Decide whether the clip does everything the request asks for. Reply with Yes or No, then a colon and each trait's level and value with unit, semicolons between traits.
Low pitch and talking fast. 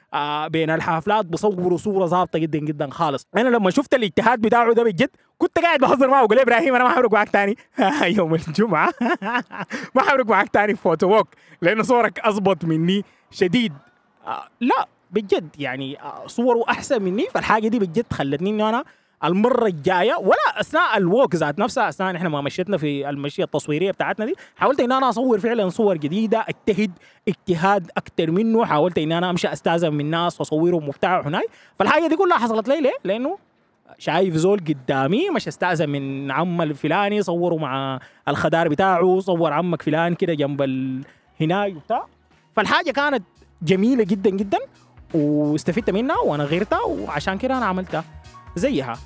No: high, 190 Hz; fast, 155 wpm